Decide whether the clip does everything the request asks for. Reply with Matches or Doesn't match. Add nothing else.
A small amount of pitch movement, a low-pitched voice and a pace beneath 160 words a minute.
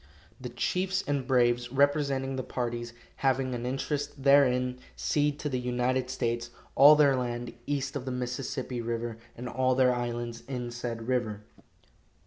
Matches